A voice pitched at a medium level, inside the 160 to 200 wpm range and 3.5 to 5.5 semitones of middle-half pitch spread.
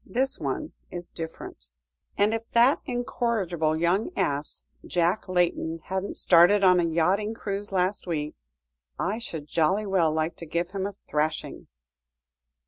No: medium, 180 Hz; average, 140 wpm; average, 4.0 semitones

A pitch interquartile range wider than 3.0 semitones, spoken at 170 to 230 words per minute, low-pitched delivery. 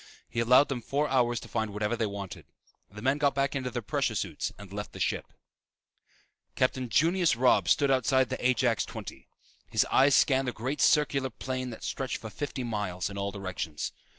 Yes: average, 4.0 semitones; average, 190 wpm; low, 125 Hz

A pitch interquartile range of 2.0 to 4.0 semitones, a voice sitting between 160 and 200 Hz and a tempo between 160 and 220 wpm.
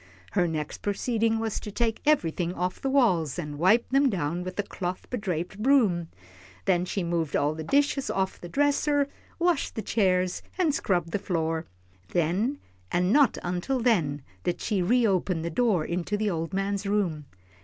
No: average, 5.2 semitones; high, 190 Hz; average, 170 wpm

